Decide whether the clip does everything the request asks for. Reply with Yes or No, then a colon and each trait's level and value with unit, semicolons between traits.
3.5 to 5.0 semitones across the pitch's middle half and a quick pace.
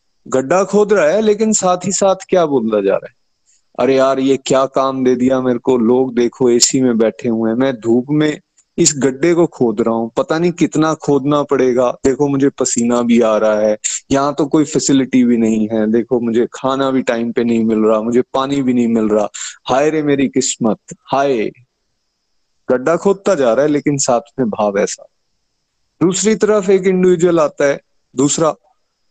Yes: average, 4.5 semitones; fast, 195 wpm